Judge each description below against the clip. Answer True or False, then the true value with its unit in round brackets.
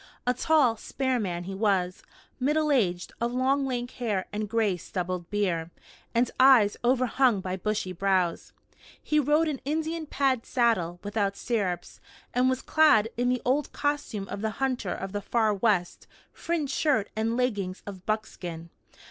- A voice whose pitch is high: True (225 Hz)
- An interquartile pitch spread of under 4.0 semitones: False (5.2 semitones)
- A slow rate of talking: False (155 wpm)